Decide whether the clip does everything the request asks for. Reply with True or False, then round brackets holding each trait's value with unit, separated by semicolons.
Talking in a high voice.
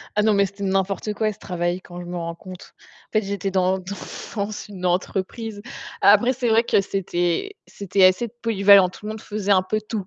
True (200 Hz)